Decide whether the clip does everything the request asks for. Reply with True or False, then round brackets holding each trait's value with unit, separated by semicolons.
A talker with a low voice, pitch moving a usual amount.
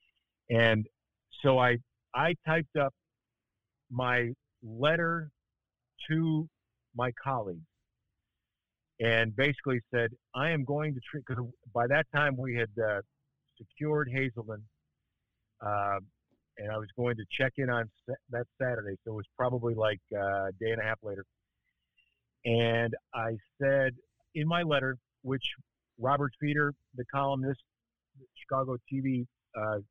True (120 Hz; 3.8 semitones)